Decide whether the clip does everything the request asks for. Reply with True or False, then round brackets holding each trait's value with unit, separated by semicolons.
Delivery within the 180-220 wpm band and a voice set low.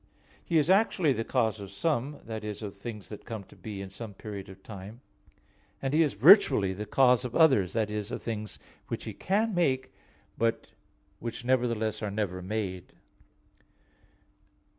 False (170 wpm; 110 Hz)